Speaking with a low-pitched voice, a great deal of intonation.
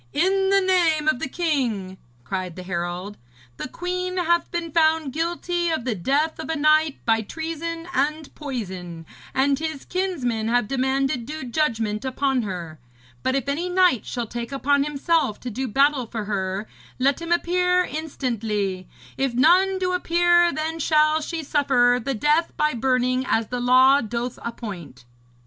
No: very high, 275 Hz; wide, 5.9 semitones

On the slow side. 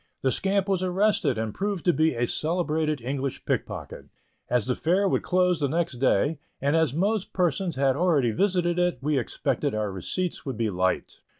No: average, 185 wpm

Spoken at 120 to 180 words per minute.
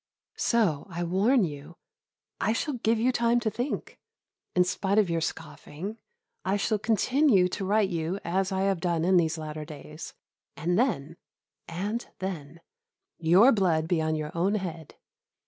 Yes: average, 165 wpm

